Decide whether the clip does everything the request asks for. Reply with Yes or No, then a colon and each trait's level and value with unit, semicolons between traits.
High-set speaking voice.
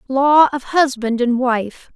Yes: very high, 260 Hz